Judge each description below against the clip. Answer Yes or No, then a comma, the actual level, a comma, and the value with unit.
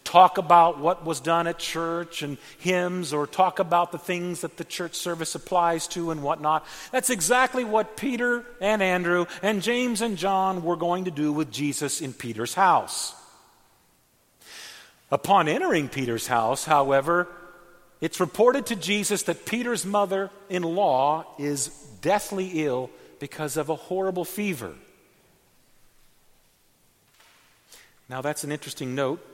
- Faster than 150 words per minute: No, average, 140 wpm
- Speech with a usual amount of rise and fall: Yes, average, 4.1 semitones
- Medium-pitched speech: Yes, medium, 175 Hz